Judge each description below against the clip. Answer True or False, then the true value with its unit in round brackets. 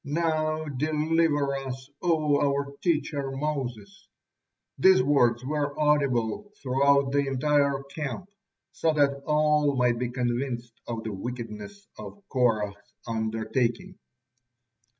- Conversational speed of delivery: False (110 wpm)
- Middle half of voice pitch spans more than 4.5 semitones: False (3.6 semitones)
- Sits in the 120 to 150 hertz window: True (140 Hz)